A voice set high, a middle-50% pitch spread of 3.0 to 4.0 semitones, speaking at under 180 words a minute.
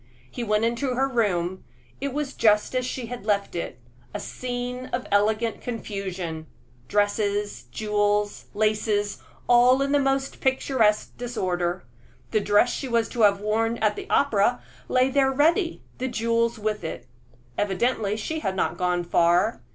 Yes: high, 220 Hz; average, 3.5 semitones; average, 150 wpm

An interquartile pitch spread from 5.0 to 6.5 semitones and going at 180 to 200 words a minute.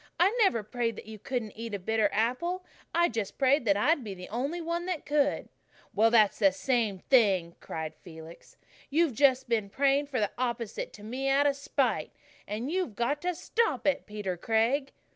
Yes: wide, 5.4 semitones; average, 190 wpm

